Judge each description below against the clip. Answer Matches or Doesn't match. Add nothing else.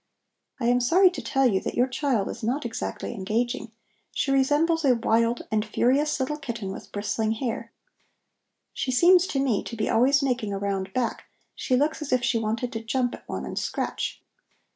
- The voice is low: Doesn't match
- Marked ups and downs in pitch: Doesn't match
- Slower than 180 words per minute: Doesn't match